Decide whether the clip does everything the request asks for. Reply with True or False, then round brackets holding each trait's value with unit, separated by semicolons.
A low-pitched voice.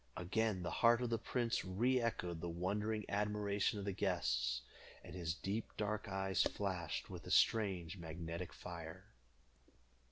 True (95 Hz)